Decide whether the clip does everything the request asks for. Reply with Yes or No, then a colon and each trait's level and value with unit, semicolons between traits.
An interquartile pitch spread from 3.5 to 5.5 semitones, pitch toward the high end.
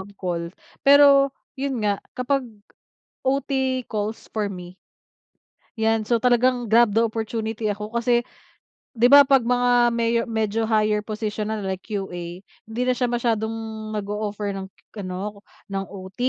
No: average, 3.0 semitones; high, 220 Hz